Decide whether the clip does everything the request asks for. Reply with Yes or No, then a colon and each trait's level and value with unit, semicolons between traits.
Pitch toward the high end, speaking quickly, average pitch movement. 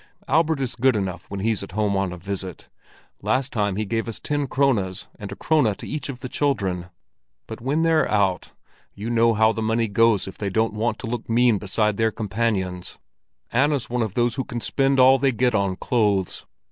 No: low, 110 Hz; fast, 210 wpm; average, 4.1 semitones